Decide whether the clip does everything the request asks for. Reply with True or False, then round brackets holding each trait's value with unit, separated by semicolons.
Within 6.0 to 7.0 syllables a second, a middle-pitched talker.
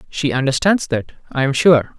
False (5.0 syllables/s; 145 Hz)